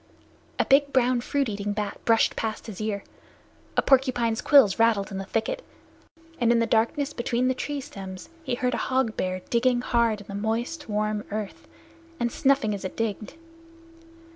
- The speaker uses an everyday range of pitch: Yes, average, 3.5 semitones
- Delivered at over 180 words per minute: No, average, 175 wpm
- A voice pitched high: Yes, high, 230 Hz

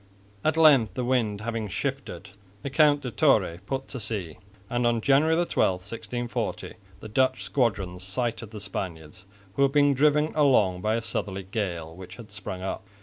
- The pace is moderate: Yes, average, 170 wpm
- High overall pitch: No, low, 115 Hz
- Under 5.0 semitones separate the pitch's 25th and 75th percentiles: No, wide, 5.6 semitones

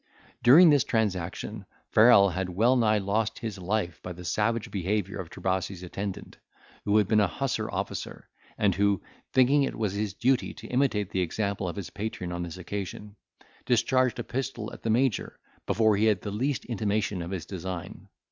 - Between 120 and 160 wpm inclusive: No, average, 180 wpm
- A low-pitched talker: Yes, low, 105 Hz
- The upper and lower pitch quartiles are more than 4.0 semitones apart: No, average, 3.3 semitones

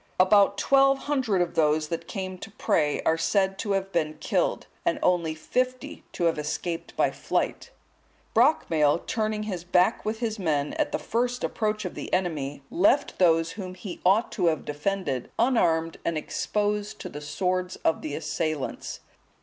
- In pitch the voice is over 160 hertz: Yes, medium, 185 Hz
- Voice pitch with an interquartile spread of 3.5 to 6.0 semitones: Yes, average, 4.7 semitones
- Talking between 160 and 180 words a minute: Yes, average, 165 wpm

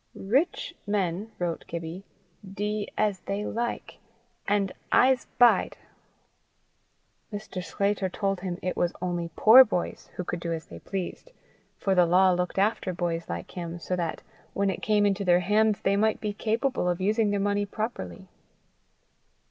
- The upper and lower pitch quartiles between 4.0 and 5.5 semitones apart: No, average, 3.1 semitones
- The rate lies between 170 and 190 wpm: No, average, 155 wpm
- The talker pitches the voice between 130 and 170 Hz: No, high, 195 Hz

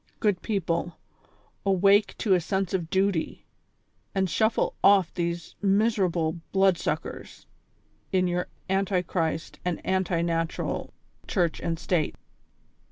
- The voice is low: No, medium, 185 Hz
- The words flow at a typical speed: No, slow, 115 wpm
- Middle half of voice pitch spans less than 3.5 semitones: Yes, narrow, 2.4 semitones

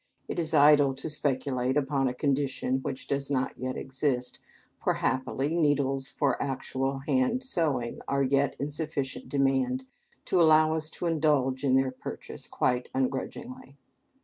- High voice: No, low, 135 Hz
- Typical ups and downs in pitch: No, narrow, 2.2 semitones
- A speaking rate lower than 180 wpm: Yes, average, 145 wpm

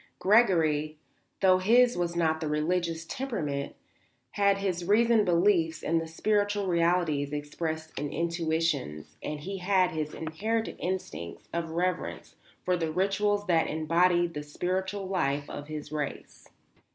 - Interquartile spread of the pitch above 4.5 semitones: No, average, 3.4 semitones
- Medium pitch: Yes, medium, 170 Hz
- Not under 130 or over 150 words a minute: Yes, slow, 135 wpm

